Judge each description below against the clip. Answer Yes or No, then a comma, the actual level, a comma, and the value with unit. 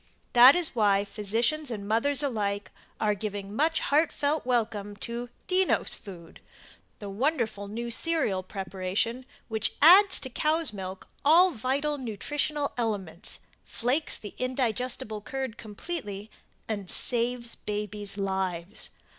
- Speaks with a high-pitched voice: Yes, high, 230 Hz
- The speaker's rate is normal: No, slow, 120 wpm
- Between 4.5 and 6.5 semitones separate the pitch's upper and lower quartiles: Yes, wide, 5.6 semitones